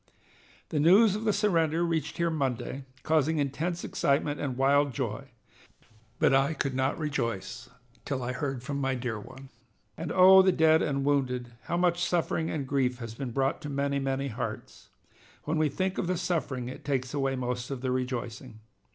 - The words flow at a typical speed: Yes, average, 180 wpm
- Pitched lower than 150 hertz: Yes, medium, 140 Hz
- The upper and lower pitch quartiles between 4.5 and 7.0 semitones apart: No, average, 3.8 semitones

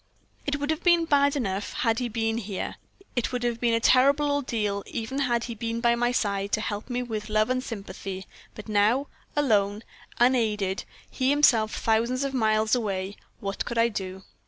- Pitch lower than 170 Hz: No, high, 230 Hz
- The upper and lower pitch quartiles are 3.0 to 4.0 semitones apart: Yes, average, 3.4 semitones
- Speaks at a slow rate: No, average, 185 wpm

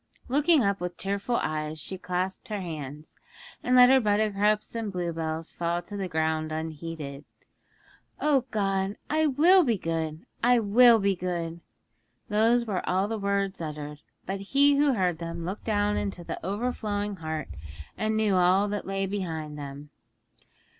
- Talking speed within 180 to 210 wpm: No, average, 155 wpm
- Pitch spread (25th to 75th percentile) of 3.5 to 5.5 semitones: Yes, average, 4.7 semitones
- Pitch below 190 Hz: No, high, 195 Hz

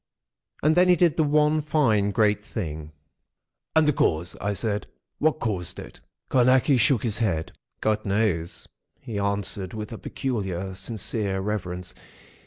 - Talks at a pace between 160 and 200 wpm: No, average, 145 wpm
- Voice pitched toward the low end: Yes, low, 105 Hz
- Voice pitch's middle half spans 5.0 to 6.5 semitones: Yes, wide, 5.4 semitones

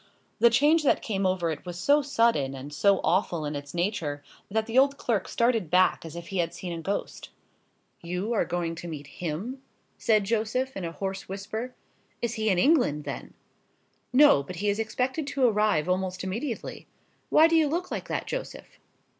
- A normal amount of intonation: No, wide, 6.0 semitones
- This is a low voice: No, high, 200 Hz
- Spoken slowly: No, average, 190 wpm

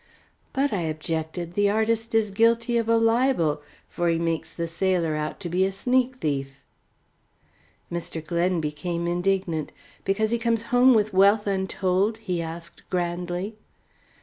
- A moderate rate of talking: Yes, average, 150 wpm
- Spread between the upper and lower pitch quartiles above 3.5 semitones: Yes, average, 4.8 semitones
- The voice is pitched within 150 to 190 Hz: Yes, medium, 185 Hz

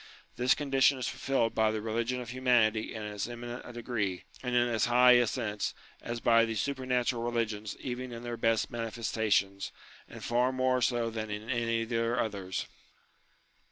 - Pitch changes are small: Yes, narrow, 2.0 semitones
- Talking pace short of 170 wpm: No, average, 180 wpm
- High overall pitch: No, low, 120 Hz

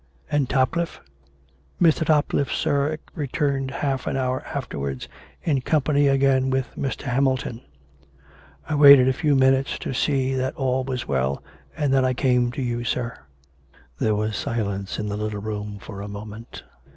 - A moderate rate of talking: Yes, average, 165 wpm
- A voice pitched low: Yes, low, 130 Hz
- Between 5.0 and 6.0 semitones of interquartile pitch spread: No, average, 4.4 semitones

